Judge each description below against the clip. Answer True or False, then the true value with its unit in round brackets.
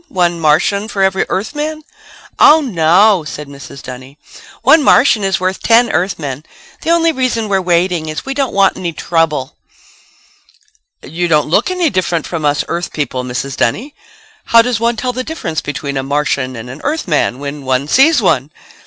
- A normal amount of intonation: False (7.9 semitones)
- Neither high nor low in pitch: True (175 Hz)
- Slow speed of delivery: False (170 wpm)